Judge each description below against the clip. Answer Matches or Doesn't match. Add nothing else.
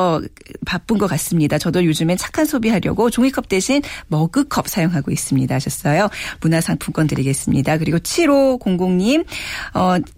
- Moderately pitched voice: Matches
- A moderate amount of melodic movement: Doesn't match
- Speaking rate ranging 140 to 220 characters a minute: Doesn't match